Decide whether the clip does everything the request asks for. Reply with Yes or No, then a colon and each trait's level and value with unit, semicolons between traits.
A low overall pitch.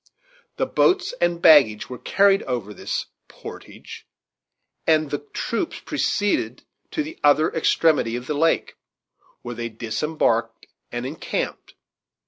No: medium, 150 Hz